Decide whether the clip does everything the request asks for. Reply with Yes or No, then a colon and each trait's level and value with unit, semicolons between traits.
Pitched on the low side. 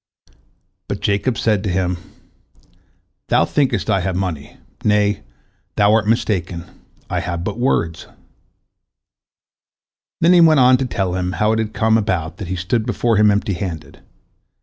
Yes: low, 100 Hz